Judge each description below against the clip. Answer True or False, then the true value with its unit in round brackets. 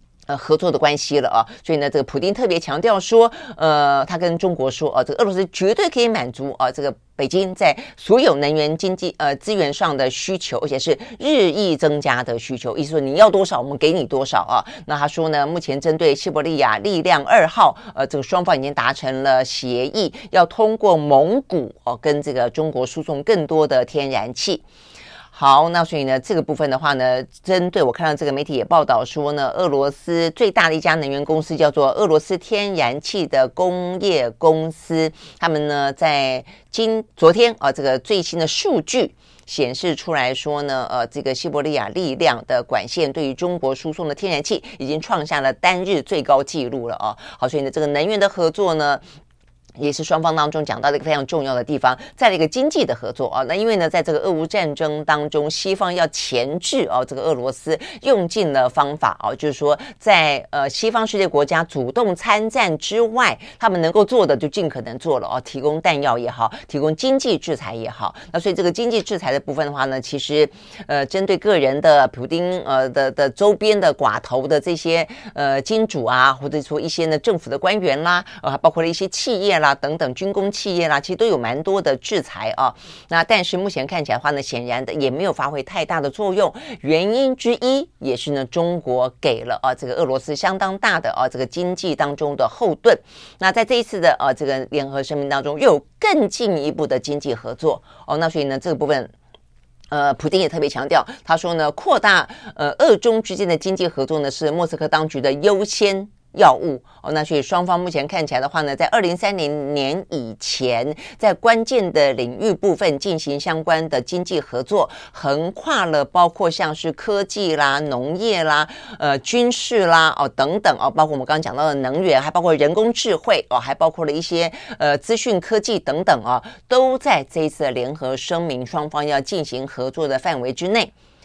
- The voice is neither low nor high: True (155 Hz)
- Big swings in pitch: False (4.9 semitones)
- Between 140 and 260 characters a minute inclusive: False (305 characters per minute)